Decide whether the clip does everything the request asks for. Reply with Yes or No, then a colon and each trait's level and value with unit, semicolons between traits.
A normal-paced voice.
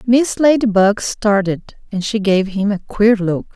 Yes: average, 170 wpm